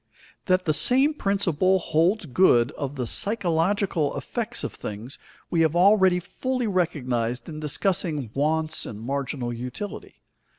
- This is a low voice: No, medium, 160 Hz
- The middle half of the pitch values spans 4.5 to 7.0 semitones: Yes, wide, 5.6 semitones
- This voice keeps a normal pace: No, slow, 130 wpm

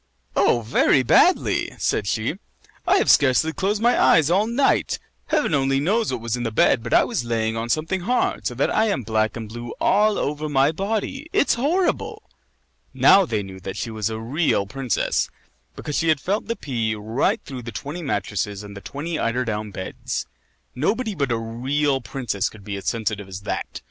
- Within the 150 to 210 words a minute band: Yes, average, 195 wpm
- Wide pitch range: Yes, wide, 7.8 semitones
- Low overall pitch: Yes, low, 130 Hz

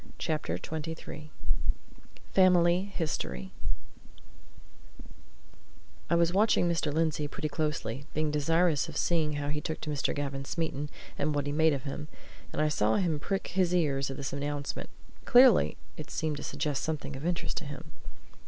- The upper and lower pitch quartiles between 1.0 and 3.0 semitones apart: Yes, narrow, 2.5 semitones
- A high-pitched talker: No, medium, 150 Hz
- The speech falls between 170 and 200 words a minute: No, average, 155 wpm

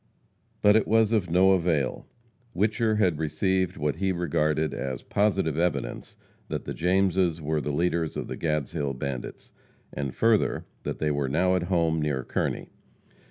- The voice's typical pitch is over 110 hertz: No, very low, 85 Hz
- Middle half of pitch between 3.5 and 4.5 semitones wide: Yes, average, 4.1 semitones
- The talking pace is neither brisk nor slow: Yes, average, 160 wpm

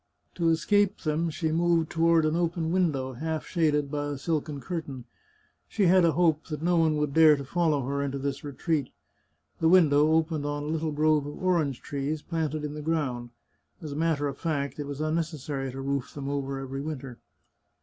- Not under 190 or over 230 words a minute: Yes, average, 200 wpm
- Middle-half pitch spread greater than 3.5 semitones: No, narrow, 2.5 semitones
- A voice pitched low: No, medium, 150 Hz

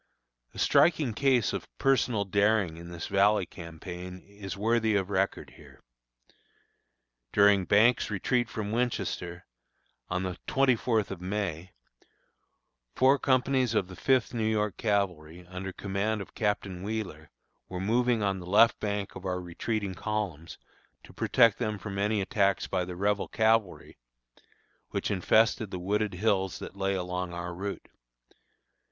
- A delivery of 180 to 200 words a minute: No, average, 145 wpm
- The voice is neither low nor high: No, low, 100 Hz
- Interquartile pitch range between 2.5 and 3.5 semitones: Yes, average, 3.2 semitones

